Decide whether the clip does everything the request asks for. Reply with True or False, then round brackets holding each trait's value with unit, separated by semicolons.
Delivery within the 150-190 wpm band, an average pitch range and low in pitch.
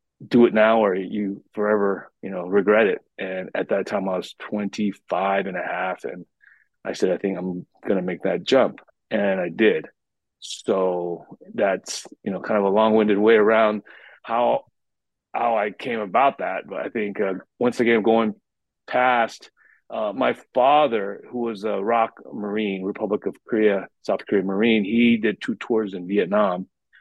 False (170 wpm; 2.3 semitones; 105 Hz)